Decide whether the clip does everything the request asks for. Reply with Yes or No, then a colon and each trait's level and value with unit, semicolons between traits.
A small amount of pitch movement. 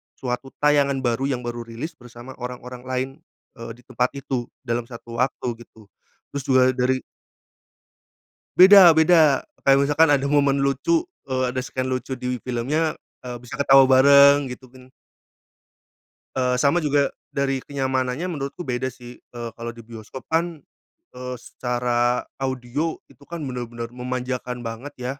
Yes: narrow, 2.3 semitones